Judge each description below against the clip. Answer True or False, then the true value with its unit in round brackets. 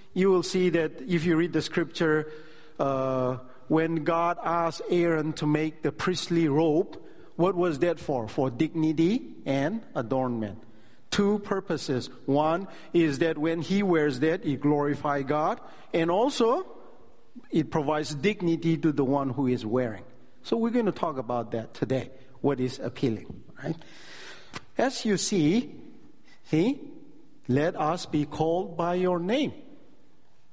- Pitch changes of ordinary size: True (4.0 semitones)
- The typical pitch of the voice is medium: True (160 Hz)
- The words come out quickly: False (145 wpm)